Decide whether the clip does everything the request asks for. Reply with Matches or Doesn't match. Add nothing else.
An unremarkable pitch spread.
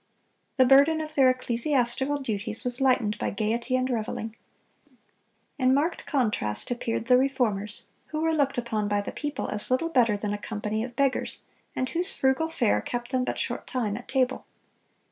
Matches